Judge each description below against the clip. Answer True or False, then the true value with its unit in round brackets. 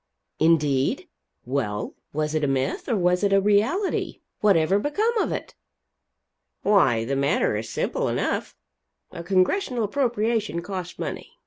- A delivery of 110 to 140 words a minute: True (135 wpm)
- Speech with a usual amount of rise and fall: False (6.8 semitones)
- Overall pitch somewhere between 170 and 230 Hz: True (185 Hz)